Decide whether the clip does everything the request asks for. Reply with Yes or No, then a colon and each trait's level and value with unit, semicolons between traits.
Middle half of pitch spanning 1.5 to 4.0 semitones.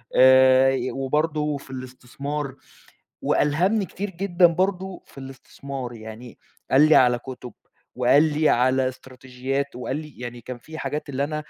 Yes: average, 3.1 semitones